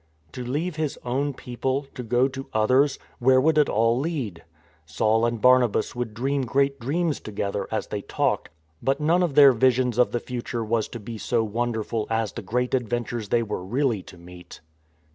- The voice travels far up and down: No, average, 3.3 semitones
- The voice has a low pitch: Yes, low, 120 Hz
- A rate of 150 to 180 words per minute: No, average, 190 wpm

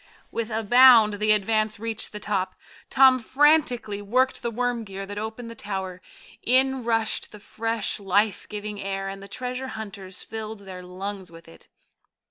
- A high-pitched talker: Yes, high, 215 Hz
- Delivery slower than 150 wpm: No, average, 165 wpm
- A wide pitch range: No, average, 3.1 semitones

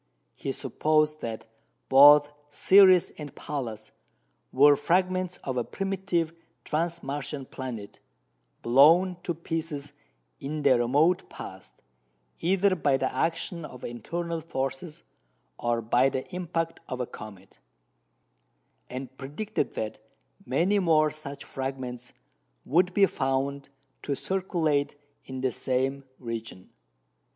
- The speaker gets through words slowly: Yes, slow, 115 wpm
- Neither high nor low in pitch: Yes, medium, 145 Hz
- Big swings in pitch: No, average, 4.5 semitones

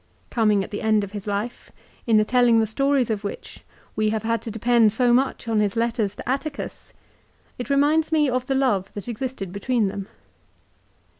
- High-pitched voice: Yes, high, 230 Hz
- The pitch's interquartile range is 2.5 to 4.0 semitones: Yes, average, 3.3 semitones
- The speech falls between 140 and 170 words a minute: No, average, 195 wpm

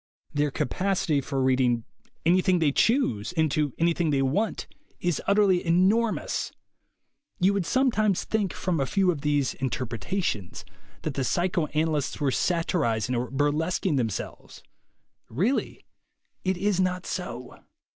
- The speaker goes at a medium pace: No, slow, 130 wpm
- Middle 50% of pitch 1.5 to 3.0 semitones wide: No, wide, 5.6 semitones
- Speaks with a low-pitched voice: No, medium, 160 Hz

